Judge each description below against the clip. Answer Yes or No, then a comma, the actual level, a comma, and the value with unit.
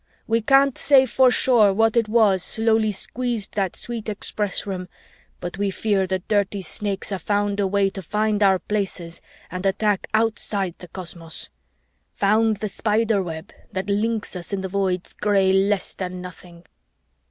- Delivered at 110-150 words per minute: No, average, 160 wpm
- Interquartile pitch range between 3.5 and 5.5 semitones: No, narrow, 2.5 semitones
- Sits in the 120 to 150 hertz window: No, high, 200 Hz